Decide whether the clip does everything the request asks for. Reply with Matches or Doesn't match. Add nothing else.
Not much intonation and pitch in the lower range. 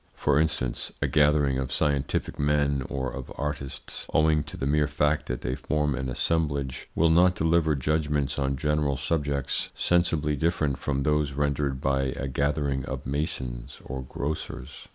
Matches